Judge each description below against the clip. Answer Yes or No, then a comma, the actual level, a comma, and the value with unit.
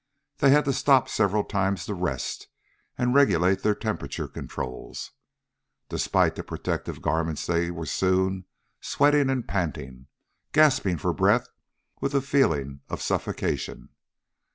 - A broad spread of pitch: Yes, wide, 8.2 semitones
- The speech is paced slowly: Yes, slow, 130 wpm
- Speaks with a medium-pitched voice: No, very low, 95 Hz